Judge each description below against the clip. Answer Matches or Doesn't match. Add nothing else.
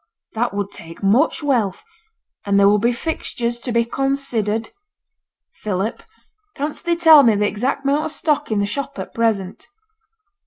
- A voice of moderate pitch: Doesn't match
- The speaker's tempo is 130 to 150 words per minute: Doesn't match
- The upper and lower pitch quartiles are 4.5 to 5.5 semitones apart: Matches